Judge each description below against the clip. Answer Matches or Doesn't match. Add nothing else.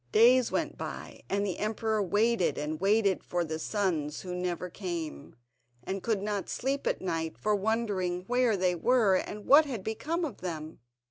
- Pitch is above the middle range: Matches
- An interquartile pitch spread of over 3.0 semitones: Matches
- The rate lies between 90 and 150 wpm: Doesn't match